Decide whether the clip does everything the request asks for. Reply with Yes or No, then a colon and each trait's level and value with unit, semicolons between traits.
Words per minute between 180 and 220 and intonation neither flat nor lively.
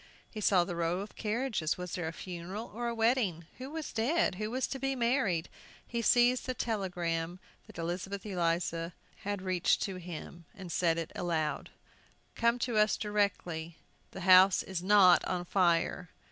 No: average, 165 wpm; average, 4.6 semitones